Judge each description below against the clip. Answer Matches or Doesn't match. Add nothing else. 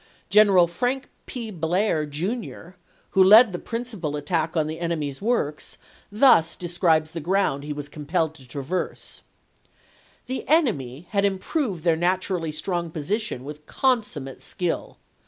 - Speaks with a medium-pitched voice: Matches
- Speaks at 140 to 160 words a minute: Matches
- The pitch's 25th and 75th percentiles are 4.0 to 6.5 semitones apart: Matches